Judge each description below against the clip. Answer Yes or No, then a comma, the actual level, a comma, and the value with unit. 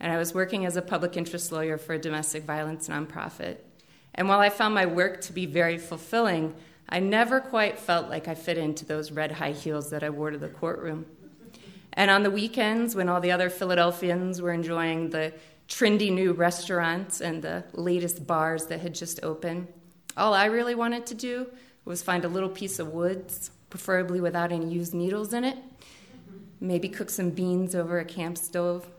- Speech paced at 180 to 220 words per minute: Yes, average, 195 wpm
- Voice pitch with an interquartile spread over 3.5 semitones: No, narrow, 2.5 semitones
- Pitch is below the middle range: No, medium, 175 Hz